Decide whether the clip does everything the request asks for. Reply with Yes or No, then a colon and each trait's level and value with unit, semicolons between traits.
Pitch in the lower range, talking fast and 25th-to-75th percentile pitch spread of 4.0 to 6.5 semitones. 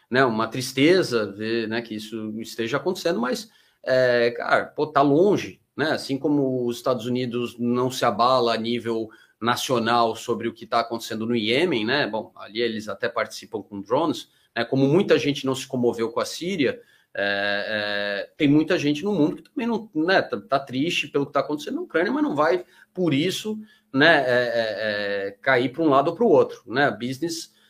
Yes: low, 125 Hz; fast, 195 wpm; average, 4.7 semitones